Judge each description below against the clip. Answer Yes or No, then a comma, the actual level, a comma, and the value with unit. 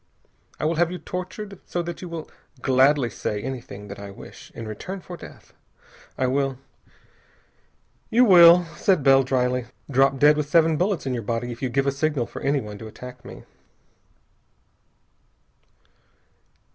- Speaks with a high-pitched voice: No, low, 135 Hz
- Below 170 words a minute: Yes, average, 160 wpm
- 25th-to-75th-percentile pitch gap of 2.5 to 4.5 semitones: No, wide, 5.4 semitones